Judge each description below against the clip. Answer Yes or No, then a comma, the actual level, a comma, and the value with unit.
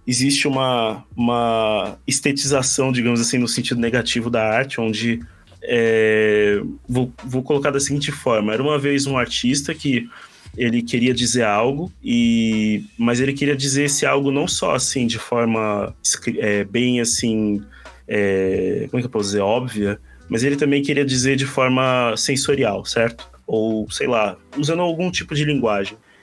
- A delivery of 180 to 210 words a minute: No, average, 160 wpm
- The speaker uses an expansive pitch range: No, average, 4.1 semitones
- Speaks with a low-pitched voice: Yes, low, 125 Hz